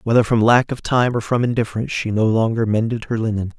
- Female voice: No, male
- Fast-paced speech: Yes, fast, 235 wpm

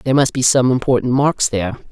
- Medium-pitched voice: No, low, 125 Hz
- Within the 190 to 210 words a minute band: No, fast, 220 wpm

